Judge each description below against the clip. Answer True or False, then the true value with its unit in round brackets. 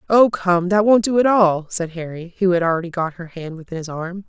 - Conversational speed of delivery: False (250 wpm)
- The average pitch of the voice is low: False (180 Hz)